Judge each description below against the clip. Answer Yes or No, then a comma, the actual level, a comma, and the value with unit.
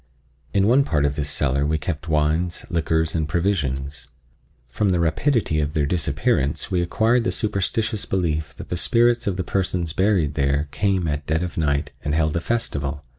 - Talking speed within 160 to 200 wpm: Yes, average, 180 wpm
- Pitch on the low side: Yes, very low, 80 Hz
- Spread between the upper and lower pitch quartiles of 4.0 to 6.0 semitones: Yes, average, 4.7 semitones